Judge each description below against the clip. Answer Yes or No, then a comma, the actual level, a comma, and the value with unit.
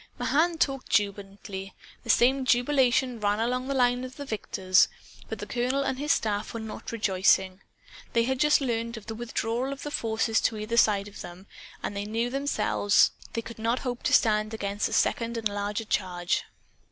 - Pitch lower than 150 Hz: No, high, 230 Hz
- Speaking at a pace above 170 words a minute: Yes, average, 190 wpm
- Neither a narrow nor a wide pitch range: Yes, average, 3.6 semitones